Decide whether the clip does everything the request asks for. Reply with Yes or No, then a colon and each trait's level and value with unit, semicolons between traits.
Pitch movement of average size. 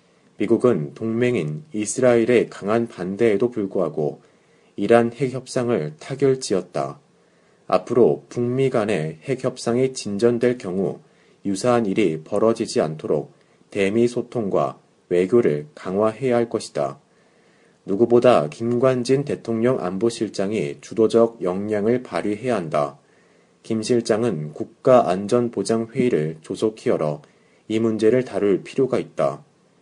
Yes: average, 3.4 semitones